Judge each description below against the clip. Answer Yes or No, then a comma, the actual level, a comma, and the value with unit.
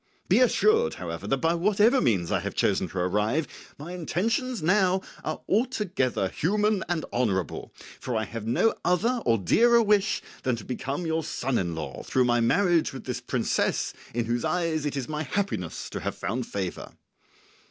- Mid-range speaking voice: Yes, medium, 155 Hz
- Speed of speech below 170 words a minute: No, average, 175 wpm